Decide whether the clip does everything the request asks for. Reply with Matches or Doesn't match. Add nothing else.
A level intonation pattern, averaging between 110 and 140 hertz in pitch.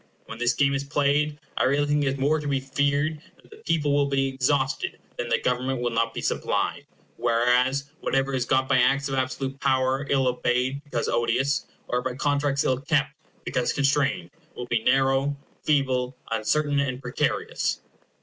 Matches